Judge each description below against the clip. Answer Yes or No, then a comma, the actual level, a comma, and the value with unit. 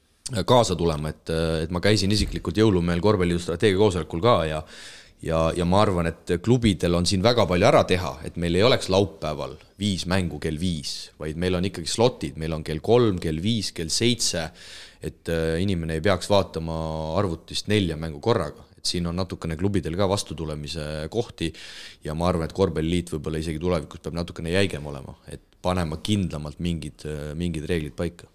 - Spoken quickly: No, average, 175 wpm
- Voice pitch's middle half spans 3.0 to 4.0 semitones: Yes, average, 3.3 semitones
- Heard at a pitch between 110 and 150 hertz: No, very low, 85 Hz